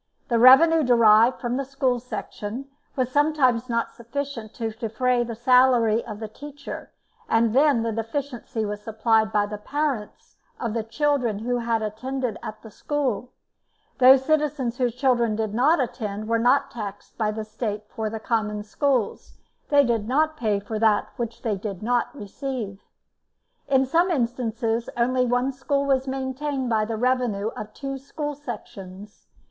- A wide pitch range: No, average, 3.5 semitones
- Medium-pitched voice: No, high, 240 Hz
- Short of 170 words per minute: Yes, average, 160 wpm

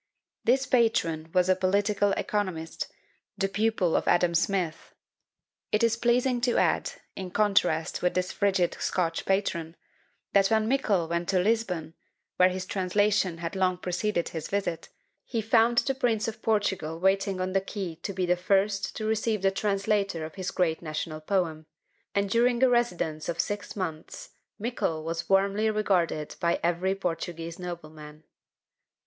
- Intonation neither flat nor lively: Yes, average, 3.8 semitones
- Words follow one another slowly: No, average, 155 wpm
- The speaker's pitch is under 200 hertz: Yes, high, 190 Hz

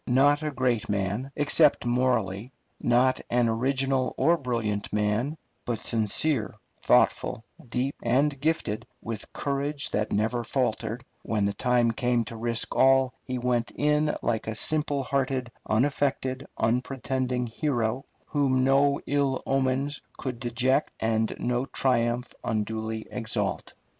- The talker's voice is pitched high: No, low, 125 Hz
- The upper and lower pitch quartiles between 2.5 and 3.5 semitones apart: Yes, average, 3.2 semitones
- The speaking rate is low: Yes, slow, 130 wpm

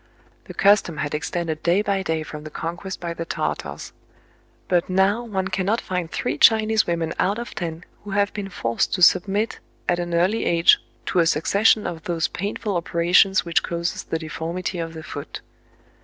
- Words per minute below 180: No, average, 185 wpm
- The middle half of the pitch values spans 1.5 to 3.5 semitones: Yes, average, 3.0 semitones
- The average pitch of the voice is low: No, medium, 175 Hz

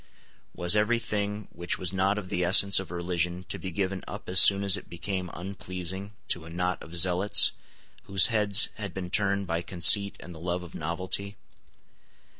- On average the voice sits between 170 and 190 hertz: No, very low, 95 Hz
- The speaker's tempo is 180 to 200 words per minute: Yes, average, 185 wpm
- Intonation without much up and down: Yes, narrow, 2.2 semitones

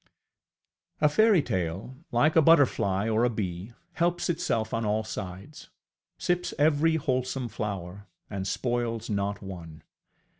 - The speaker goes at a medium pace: No, slow, 125 wpm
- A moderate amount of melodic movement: No, wide, 7.0 semitones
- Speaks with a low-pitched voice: Yes, low, 115 Hz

